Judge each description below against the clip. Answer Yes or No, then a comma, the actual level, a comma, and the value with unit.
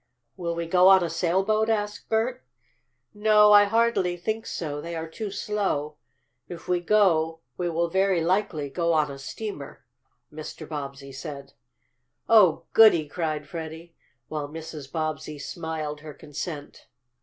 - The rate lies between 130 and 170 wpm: Yes, average, 145 wpm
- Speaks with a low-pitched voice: No, medium, 170 Hz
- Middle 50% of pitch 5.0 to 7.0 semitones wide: No, average, 4.4 semitones